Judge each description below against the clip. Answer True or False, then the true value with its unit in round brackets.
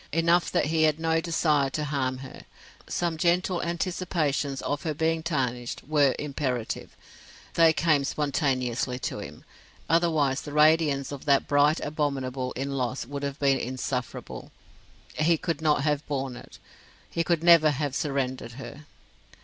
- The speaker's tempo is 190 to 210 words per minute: False (150 wpm)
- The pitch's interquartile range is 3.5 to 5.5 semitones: False (3.1 semitones)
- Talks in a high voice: False (145 Hz)